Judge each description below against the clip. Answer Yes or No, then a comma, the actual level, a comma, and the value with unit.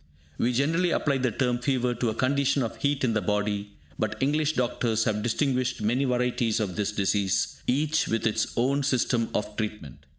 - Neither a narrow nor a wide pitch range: Yes, average, 4.0 semitones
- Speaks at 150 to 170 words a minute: No, average, 185 wpm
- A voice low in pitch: Yes, low, 120 Hz